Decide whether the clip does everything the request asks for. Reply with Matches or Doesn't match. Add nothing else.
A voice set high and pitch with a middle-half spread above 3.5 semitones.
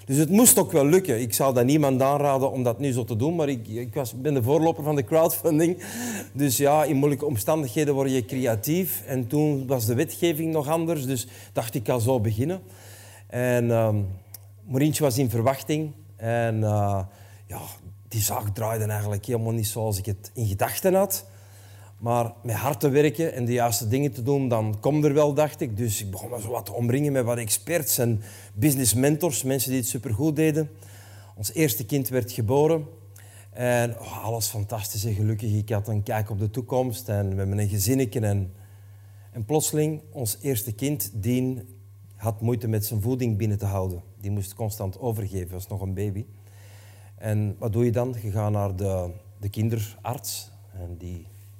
Doesn't match